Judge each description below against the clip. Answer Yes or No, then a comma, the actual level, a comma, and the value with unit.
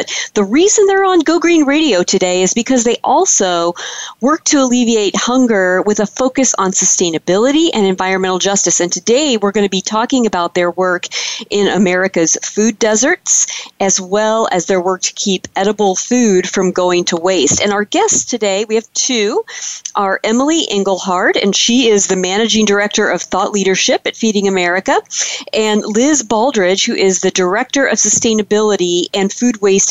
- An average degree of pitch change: Yes, average, 4.6 semitones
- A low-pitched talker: No, high, 210 Hz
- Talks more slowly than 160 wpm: No, average, 175 wpm